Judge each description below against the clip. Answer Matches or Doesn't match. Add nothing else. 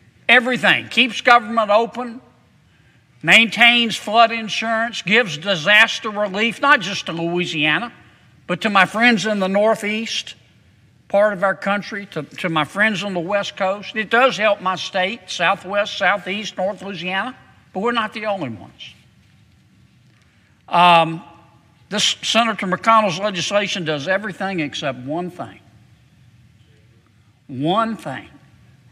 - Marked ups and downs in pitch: Matches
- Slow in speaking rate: Matches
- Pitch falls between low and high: Doesn't match